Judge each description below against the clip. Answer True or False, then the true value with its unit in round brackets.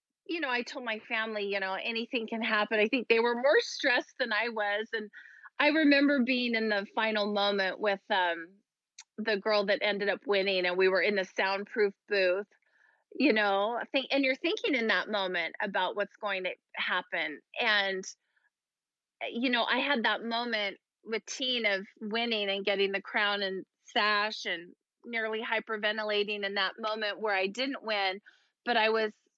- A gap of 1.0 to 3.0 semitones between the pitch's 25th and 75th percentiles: True (2.7 semitones)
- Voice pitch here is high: True (210 Hz)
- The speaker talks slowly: False (180 wpm)